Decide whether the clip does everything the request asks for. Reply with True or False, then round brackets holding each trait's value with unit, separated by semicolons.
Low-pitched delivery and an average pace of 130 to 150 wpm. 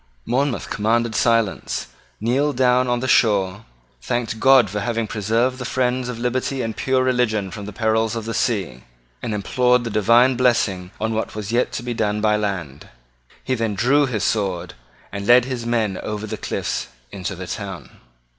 False (115 Hz; 180 wpm)